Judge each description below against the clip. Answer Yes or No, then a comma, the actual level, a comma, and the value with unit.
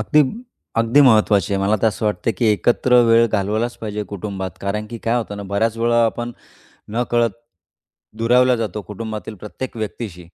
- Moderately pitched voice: No, low, 110 Hz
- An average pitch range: No, narrow, 2.3 semitones